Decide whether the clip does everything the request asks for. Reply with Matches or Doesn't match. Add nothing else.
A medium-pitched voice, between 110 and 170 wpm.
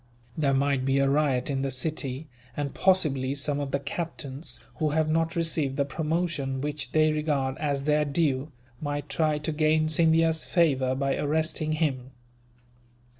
Matches